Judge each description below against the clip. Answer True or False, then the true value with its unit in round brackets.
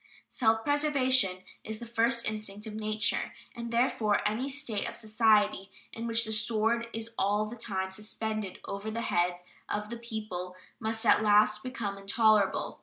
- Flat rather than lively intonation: True (2.0 semitones)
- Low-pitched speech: False (220 Hz)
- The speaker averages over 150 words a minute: True (160 wpm)